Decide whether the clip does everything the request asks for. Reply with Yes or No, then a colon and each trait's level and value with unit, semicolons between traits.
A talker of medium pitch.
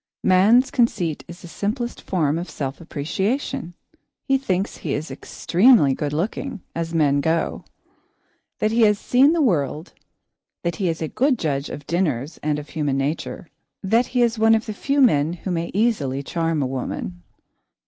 Yes: medium, 175 Hz